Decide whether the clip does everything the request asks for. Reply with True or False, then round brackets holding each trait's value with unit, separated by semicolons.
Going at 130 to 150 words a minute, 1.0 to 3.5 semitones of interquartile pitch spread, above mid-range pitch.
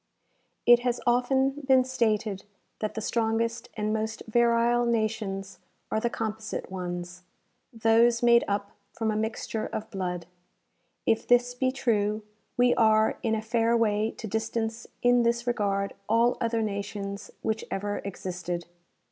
True (140 wpm; 2.4 semitones; 220 Hz)